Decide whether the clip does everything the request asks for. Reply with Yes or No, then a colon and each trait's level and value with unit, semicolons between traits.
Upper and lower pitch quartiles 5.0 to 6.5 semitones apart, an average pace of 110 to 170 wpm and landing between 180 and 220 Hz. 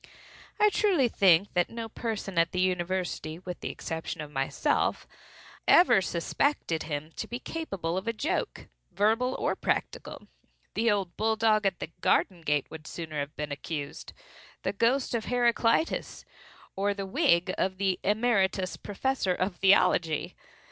Yes: average, 5.3 semitones; average, 140 wpm; high, 190 Hz